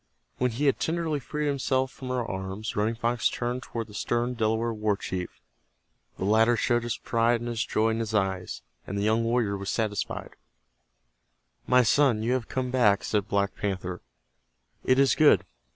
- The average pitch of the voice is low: Yes, low, 115 Hz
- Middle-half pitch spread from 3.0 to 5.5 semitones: Yes, average, 3.3 semitones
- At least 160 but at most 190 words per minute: Yes, average, 180 wpm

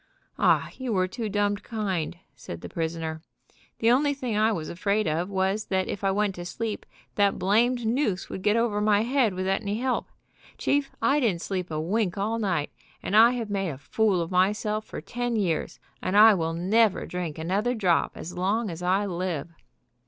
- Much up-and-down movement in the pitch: No, average, 3.7 semitones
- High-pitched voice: Yes, high, 200 Hz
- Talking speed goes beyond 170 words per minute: Yes, average, 195 wpm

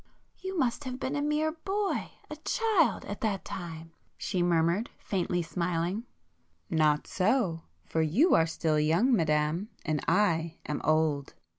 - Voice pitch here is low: No, medium, 175 Hz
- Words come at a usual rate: No, slow, 130 wpm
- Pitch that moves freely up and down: Yes, wide, 7.9 semitones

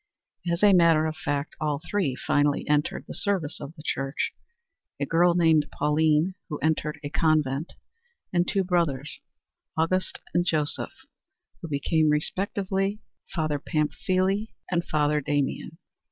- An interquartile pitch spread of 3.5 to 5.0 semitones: No, average, 3.1 semitones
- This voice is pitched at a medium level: Yes, medium, 155 Hz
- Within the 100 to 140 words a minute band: Yes, slow, 135 wpm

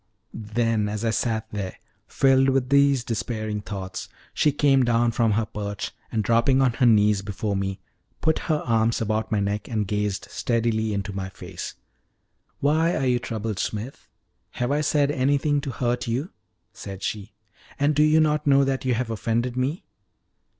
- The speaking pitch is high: No, low, 115 Hz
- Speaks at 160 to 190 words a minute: Yes, average, 170 wpm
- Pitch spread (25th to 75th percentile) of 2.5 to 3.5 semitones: No, average, 4.2 semitones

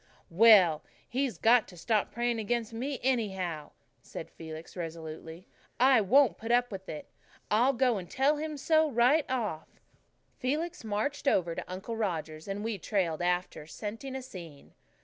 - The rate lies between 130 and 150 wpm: No, average, 160 wpm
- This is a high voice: Yes, high, 220 Hz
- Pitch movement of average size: No, wide, 6.4 semitones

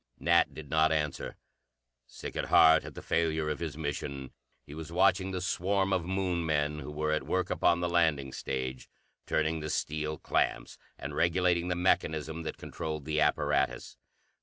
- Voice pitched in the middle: No, very low, 80 Hz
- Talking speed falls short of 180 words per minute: Yes, average, 170 wpm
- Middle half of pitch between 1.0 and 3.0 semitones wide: Yes, narrow, 2.4 semitones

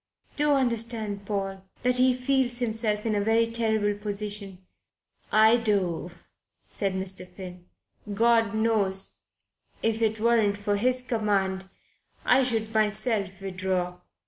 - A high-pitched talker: Yes, high, 215 Hz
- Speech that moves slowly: Yes, slow, 125 wpm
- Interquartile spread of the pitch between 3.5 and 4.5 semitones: No, average, 2.9 semitones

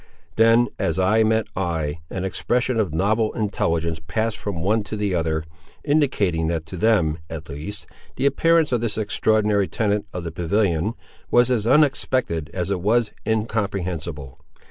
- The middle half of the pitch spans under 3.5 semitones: No, average, 5.0 semitones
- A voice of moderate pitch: No, low, 100 Hz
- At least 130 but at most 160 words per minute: Yes, average, 155 wpm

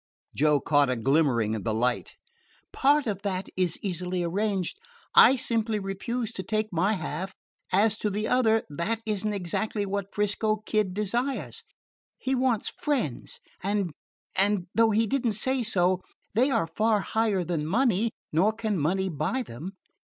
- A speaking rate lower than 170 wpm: Yes, average, 160 wpm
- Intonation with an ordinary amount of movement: Yes, average, 4.0 semitones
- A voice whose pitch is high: Yes, high, 200 Hz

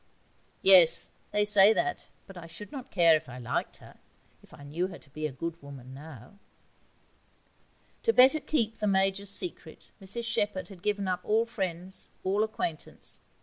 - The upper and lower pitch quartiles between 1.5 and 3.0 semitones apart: No, average, 4.3 semitones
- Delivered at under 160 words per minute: No, average, 170 wpm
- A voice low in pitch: No, high, 190 Hz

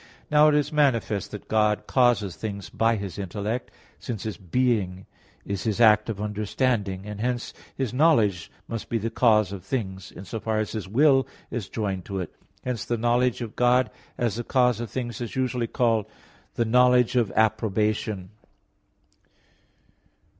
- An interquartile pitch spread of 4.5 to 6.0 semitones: No, average, 3.3 semitones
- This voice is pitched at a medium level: No, low, 110 Hz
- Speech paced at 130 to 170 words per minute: Yes, average, 165 wpm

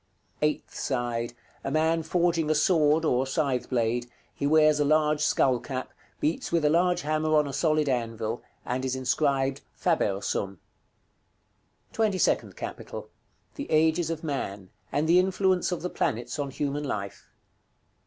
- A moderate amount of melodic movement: Yes, average, 4.0 semitones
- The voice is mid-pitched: Yes, medium, 150 Hz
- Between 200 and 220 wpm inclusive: No, average, 160 wpm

